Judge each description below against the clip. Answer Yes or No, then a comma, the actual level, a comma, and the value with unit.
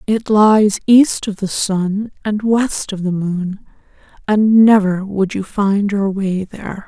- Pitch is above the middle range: Yes, high, 200 Hz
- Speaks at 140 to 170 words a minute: Yes, average, 165 wpm